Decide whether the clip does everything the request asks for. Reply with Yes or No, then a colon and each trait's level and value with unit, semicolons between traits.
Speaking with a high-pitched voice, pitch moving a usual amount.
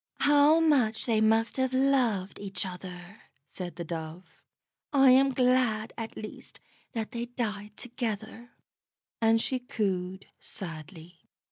Yes: high, 220 Hz; average, 5.0 semitones